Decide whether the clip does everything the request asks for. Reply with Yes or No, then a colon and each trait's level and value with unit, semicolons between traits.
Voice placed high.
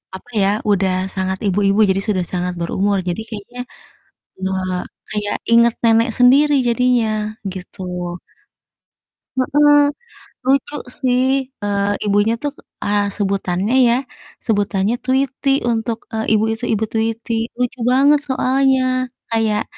Yes: high, 225 Hz